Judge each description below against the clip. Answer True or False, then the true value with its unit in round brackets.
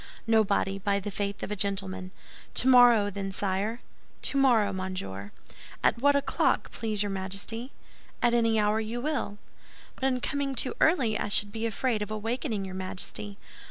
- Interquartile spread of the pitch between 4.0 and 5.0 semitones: False (3.4 semitones)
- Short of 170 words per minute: True (160 wpm)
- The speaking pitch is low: False (210 Hz)